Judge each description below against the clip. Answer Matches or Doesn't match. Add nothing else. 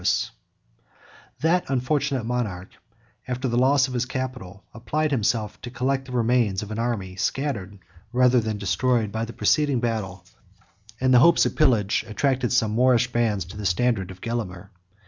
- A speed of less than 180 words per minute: Matches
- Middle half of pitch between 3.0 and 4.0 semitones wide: Matches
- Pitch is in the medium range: Doesn't match